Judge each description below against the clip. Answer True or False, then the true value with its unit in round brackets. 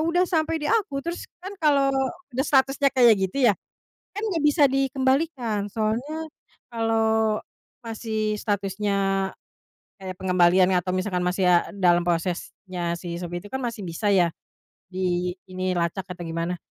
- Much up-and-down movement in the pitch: True (6.7 semitones)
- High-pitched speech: True (210 Hz)